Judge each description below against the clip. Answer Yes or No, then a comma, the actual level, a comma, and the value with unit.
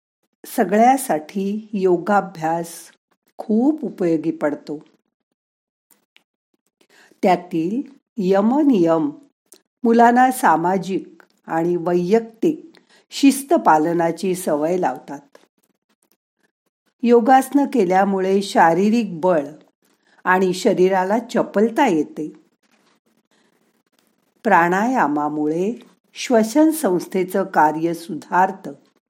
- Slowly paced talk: Yes, slow, 60 wpm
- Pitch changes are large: Yes, wide, 5.7 semitones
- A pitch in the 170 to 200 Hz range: Yes, high, 195 Hz